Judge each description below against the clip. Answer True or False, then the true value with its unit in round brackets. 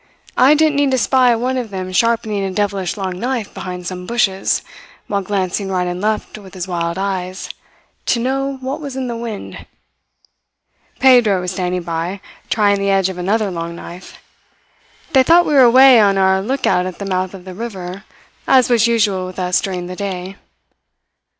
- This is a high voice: True (200 Hz)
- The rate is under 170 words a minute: False (180 wpm)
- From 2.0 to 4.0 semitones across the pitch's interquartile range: False (4.4 semitones)